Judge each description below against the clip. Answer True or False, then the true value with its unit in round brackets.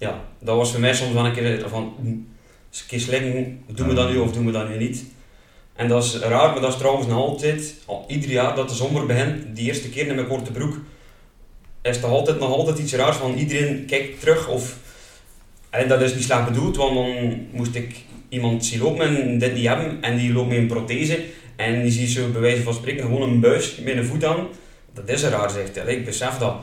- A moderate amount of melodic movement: False (2.2 semitones)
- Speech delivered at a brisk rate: True (240 wpm)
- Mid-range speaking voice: False (125 Hz)